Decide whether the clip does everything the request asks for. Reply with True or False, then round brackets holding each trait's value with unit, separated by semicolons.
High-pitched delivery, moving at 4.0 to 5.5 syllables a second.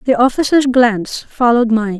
True (240 Hz; 5.4 syllables/s)